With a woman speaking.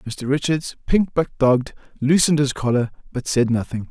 No: male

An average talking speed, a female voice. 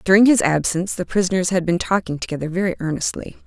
Yes: average, 190 wpm; female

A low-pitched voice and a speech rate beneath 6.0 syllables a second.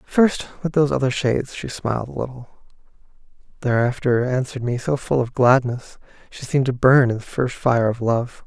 Yes: low, 130 Hz; 5.3 syllables/s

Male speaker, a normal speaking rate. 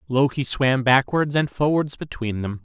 Yes: male; average, 160 wpm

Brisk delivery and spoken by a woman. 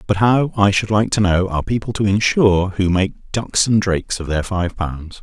No: fast, 230 wpm; male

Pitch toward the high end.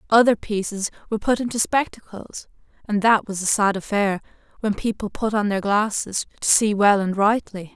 Yes: high, 210 Hz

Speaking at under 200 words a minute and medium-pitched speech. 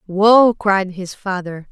No: average, 140 wpm; high, 195 Hz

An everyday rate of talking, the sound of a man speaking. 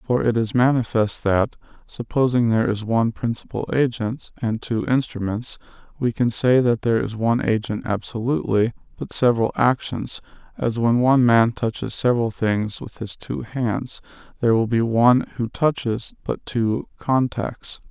Yes: average, 155 wpm; male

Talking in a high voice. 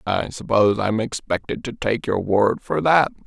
No: low, 110 Hz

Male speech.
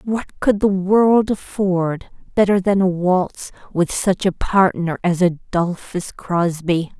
No: female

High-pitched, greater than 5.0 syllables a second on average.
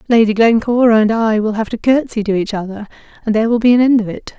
Yes: high, 225 Hz; 6.5 syllables/s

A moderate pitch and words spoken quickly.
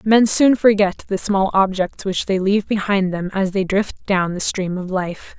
No: high, 195 Hz; fast, 210 wpm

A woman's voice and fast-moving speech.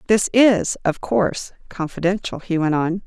No: female; average, 155 wpm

